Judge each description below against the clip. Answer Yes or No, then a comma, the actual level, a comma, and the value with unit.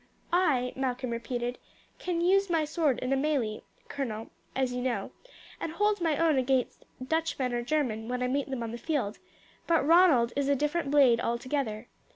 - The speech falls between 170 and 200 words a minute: Yes, average, 185 wpm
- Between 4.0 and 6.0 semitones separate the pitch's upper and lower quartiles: Yes, average, 4.3 semitones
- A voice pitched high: Yes, very high, 270 Hz